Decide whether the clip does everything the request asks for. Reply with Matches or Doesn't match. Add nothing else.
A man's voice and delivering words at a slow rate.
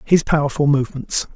Matches